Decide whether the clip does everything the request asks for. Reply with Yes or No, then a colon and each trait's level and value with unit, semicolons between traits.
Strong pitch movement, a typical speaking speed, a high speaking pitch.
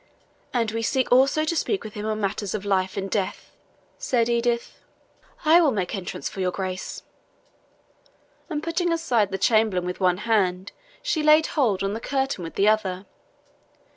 Yes: wide, 5.7 semitones; average, 170 wpm; high, 215 Hz